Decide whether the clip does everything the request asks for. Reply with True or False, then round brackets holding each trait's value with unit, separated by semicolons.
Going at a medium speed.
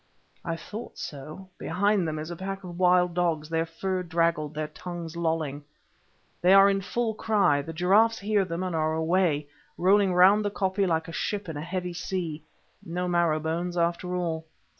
True (180 wpm)